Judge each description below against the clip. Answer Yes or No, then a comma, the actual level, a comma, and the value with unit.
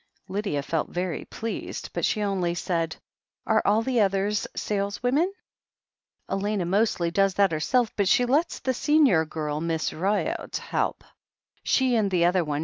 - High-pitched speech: Yes, high, 195 Hz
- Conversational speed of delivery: Yes, average, 150 wpm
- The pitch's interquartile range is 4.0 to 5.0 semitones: Yes, average, 4.5 semitones